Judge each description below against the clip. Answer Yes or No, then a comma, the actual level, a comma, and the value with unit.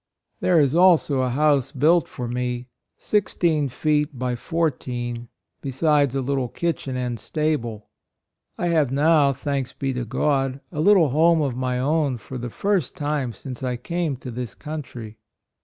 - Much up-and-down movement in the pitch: No, average, 3.8 semitones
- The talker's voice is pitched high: No, medium, 140 Hz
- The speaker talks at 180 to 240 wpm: No, average, 165 wpm